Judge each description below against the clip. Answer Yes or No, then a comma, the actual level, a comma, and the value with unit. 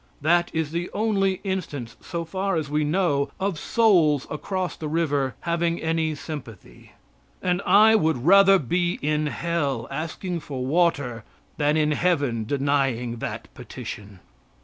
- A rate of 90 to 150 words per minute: Yes, average, 140 wpm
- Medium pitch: Yes, medium, 160 Hz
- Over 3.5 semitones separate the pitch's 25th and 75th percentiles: Yes, average, 4.0 semitones